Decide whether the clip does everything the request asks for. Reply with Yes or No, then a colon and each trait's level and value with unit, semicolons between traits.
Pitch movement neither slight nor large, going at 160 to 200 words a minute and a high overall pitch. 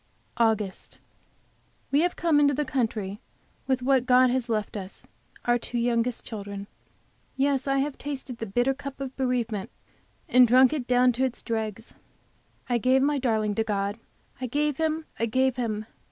Yes: average, 3.3 semitones; average, 170 wpm; very high, 250 Hz